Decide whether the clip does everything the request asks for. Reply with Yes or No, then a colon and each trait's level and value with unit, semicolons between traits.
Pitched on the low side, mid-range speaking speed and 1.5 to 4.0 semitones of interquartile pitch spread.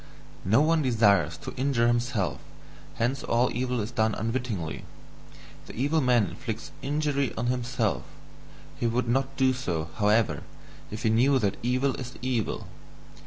Yes: low, 120 Hz; average, 145 wpm; average, 3.0 semitones